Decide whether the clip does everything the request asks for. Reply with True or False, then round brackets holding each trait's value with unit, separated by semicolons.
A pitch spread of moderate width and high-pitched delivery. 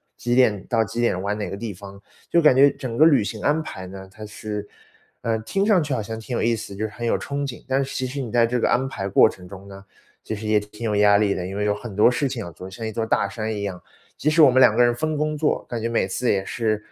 False (4.0 semitones; 110 Hz)